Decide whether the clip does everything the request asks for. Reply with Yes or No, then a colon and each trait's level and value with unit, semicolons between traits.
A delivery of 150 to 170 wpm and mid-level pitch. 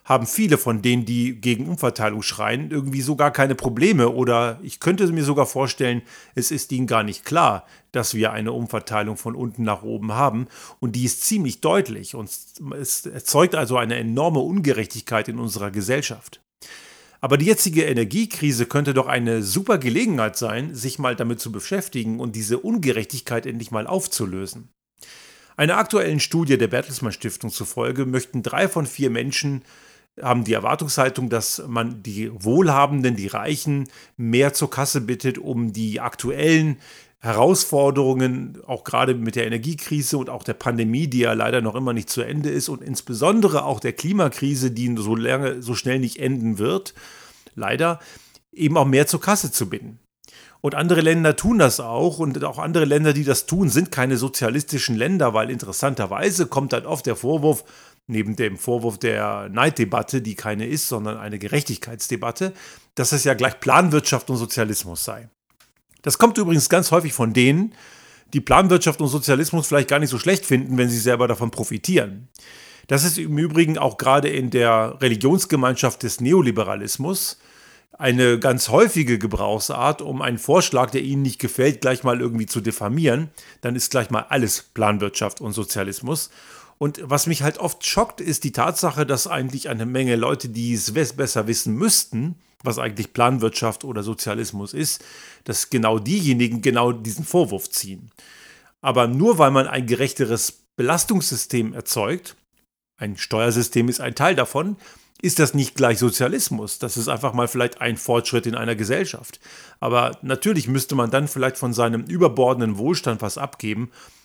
No: average, 160 wpm; low, 130 Hz